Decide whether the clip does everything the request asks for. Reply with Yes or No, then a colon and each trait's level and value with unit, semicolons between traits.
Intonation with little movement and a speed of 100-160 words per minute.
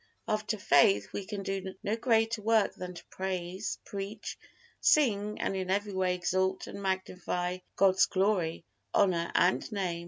Yes: narrow, 2.3 semitones; average, 150 wpm